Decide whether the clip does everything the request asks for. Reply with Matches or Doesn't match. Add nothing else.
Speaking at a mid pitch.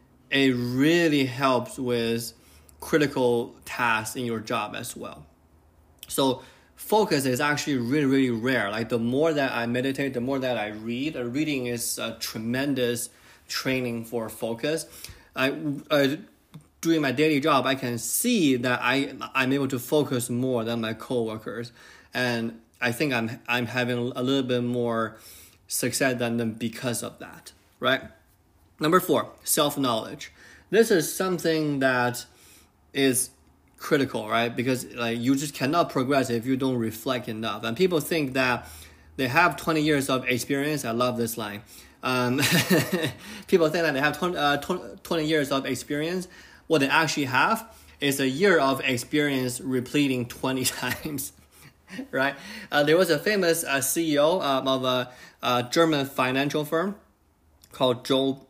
Doesn't match